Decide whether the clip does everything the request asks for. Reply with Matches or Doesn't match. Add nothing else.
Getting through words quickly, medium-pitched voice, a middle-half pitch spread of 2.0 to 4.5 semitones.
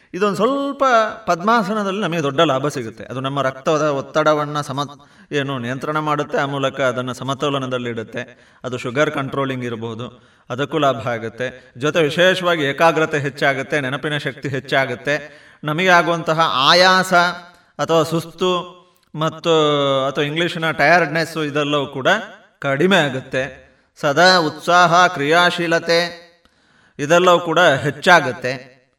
Matches